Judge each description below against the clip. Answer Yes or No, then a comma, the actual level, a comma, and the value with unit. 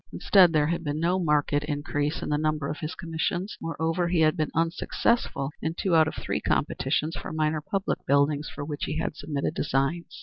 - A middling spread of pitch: No, narrow, 2.1 semitones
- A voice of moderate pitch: Yes, medium, 155 Hz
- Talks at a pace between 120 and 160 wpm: No, average, 200 wpm